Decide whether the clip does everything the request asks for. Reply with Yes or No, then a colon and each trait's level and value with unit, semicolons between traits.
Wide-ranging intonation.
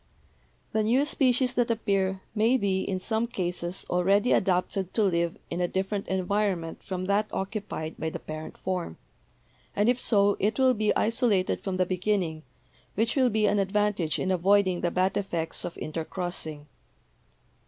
No: average, 3.1 semitones